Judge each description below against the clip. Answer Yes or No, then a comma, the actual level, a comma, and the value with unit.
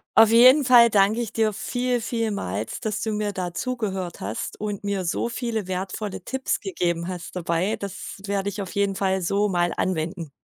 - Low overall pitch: No, high, 200 Hz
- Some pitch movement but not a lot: Yes, average, 3.5 semitones